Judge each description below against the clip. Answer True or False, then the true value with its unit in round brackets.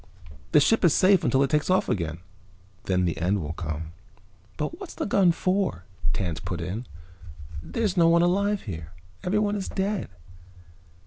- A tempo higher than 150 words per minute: True (165 wpm)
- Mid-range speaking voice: True (150 Hz)